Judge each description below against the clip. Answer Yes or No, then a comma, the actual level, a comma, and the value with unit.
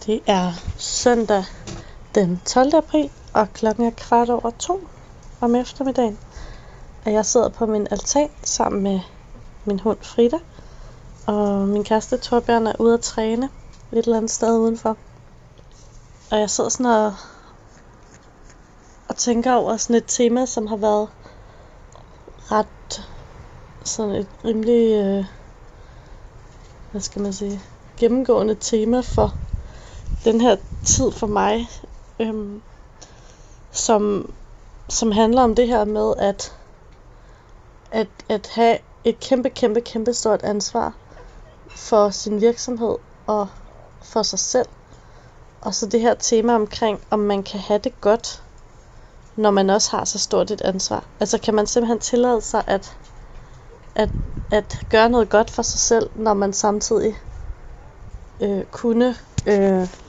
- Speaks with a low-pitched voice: No, high, 220 Hz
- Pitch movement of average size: No, narrow, 2.3 semitones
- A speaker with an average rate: No, slow, 135 wpm